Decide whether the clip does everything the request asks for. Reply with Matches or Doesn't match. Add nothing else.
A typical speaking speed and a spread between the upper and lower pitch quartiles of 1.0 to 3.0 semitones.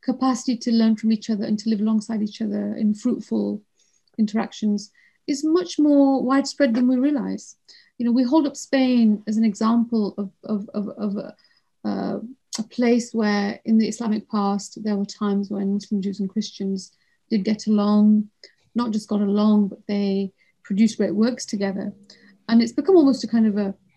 Matches